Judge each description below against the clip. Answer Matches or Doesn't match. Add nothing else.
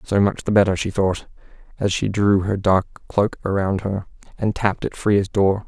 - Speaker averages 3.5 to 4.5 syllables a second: Doesn't match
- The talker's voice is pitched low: Matches